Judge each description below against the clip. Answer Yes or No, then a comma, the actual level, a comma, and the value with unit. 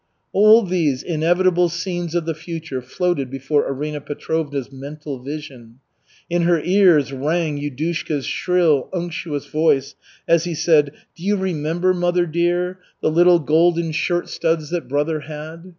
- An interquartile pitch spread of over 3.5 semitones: No, average, 3.0 semitones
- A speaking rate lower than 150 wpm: Yes, average, 140 wpm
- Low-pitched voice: No, medium, 160 Hz